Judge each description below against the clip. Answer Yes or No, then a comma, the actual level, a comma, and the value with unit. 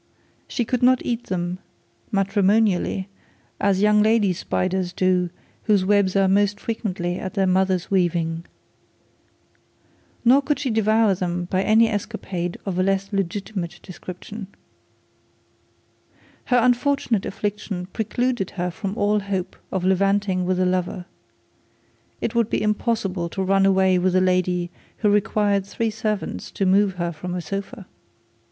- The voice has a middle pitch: No, high, 195 Hz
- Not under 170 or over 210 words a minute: No, average, 140 wpm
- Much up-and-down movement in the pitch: No, narrow, 2.5 semitones